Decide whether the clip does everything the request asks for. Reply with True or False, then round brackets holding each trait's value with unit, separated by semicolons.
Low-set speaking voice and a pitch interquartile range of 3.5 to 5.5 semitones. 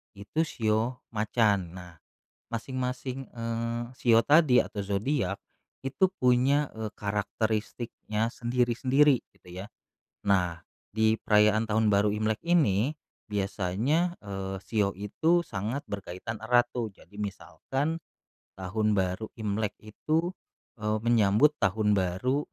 True (110 Hz; 3.8 semitones)